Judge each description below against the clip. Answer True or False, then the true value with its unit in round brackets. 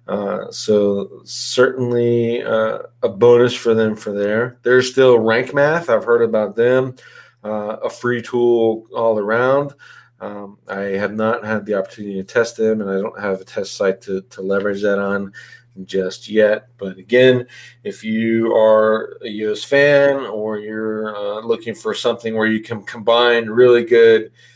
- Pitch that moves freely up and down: False (2.5 semitones)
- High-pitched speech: False (110 Hz)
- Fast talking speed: False (165 wpm)